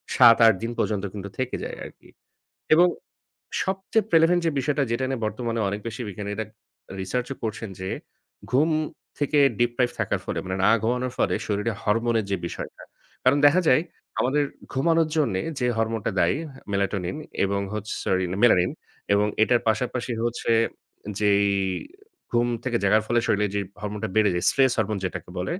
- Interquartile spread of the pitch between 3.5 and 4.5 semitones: Yes, average, 4.0 semitones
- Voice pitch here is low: Yes, low, 115 Hz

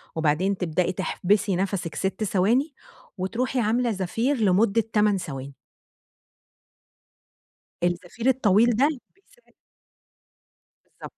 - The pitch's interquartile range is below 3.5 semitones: No, average, 4.5 semitones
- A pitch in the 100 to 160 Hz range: No, high, 200 Hz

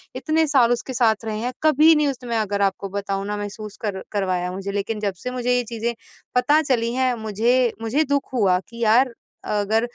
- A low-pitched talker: No, high, 230 Hz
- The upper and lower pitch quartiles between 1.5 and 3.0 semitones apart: No, average, 3.7 semitones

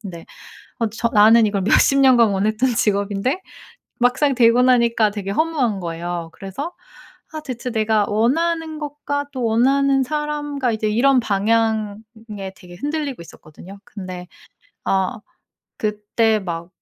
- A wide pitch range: No, average, 4.9 semitones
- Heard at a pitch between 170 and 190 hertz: No, high, 225 Hz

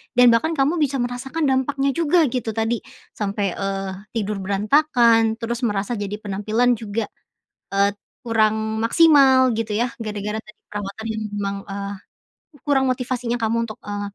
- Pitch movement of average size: Yes, average, 3.5 semitones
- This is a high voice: Yes, high, 225 Hz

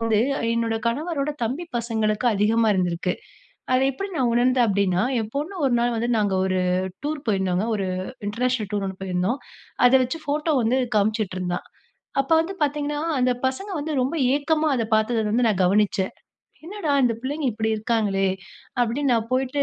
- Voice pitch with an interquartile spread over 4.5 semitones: Yes, average, 5.3 semitones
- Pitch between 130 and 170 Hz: No, high, 235 Hz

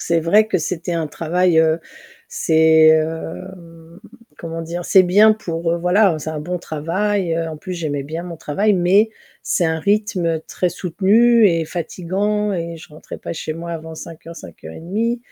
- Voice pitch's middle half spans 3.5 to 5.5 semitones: No, average, 2.8 semitones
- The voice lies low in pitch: No, medium, 170 Hz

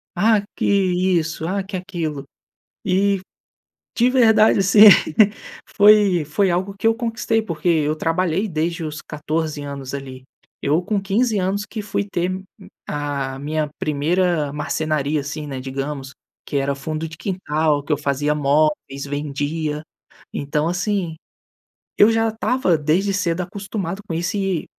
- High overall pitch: No, medium, 165 Hz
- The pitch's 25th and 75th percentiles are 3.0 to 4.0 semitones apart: No, average, 4.8 semitones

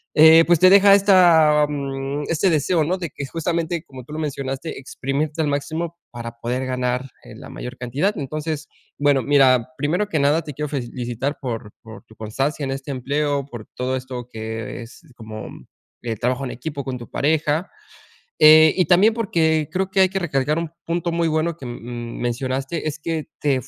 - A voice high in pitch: No, medium, 145 Hz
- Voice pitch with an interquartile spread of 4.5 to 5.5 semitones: No, average, 4.1 semitones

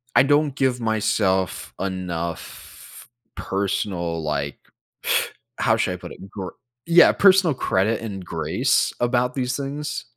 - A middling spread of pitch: No, wide, 6.4 semitones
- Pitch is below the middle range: Yes, low, 105 Hz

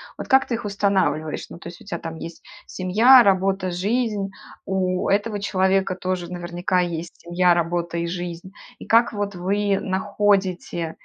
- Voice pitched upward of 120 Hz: Yes, medium, 185 Hz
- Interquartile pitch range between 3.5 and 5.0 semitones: No, narrow, 2.6 semitones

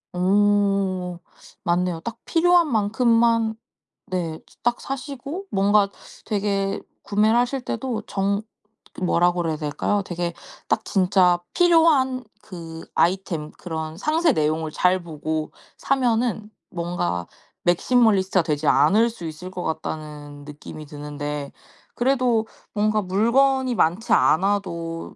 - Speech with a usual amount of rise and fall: No, wide, 5.8 semitones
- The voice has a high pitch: Yes, high, 195 Hz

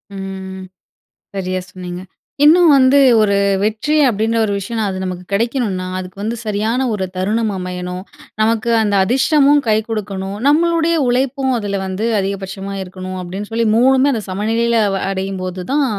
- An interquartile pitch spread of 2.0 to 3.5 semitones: No, average, 4.2 semitones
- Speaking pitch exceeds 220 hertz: No, high, 210 Hz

